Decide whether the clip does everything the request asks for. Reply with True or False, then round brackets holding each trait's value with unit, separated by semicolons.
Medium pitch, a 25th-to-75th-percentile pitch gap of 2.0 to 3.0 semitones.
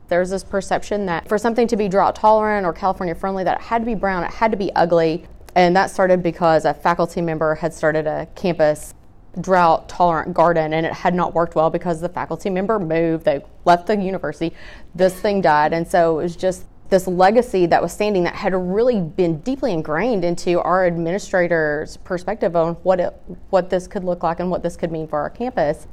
True (175 Hz; 2.6 semitones)